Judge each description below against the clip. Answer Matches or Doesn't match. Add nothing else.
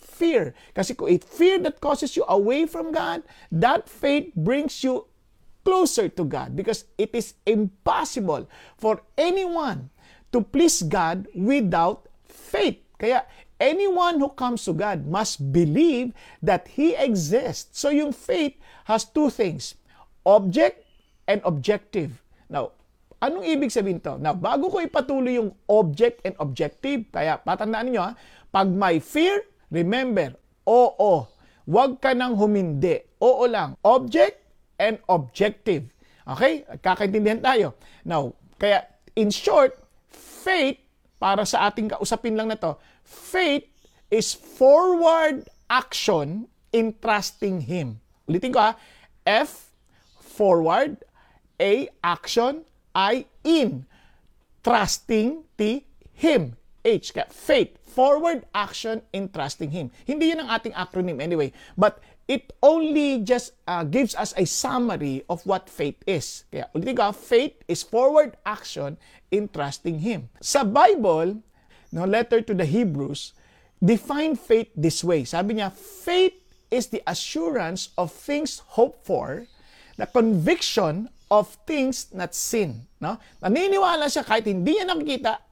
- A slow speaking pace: Matches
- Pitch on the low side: Doesn't match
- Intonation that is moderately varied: Doesn't match